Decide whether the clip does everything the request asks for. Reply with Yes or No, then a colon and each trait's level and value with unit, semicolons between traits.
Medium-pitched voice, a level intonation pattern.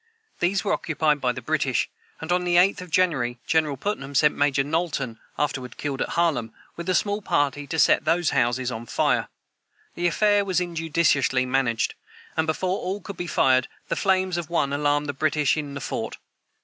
No: medium, 155 Hz; average, 4.4 semitones